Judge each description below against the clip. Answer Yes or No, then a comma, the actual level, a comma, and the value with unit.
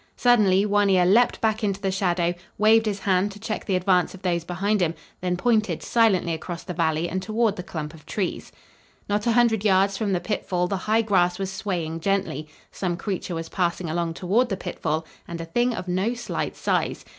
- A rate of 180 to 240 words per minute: Yes, fast, 205 wpm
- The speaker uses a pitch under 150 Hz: No, high, 190 Hz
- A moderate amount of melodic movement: Yes, average, 3.2 semitones